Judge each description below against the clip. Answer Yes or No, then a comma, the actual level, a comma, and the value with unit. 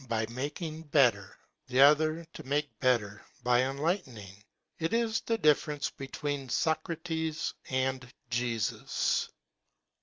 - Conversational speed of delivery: No, slow, 110 wpm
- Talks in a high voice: No, medium, 140 Hz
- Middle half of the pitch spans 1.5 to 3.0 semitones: No, average, 4.3 semitones